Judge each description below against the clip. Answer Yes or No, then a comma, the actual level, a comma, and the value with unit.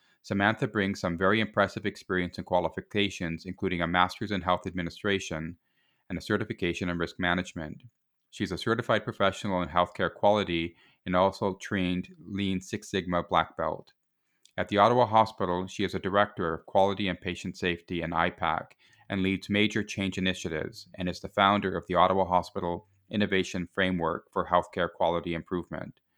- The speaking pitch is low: Yes, very low, 95 Hz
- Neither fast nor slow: Yes, average, 160 wpm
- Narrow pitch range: Yes, narrow, 2.3 semitones